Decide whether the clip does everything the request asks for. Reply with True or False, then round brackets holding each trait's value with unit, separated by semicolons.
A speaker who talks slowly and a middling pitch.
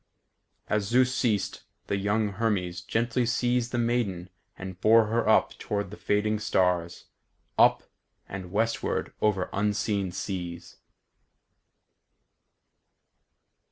False (105 wpm; 105 Hz)